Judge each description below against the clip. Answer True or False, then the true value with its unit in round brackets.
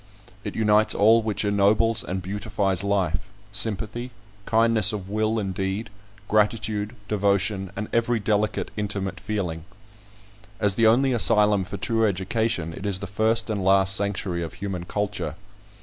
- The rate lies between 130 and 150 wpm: True (145 wpm)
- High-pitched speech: False (105 Hz)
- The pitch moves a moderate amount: False (2.2 semitones)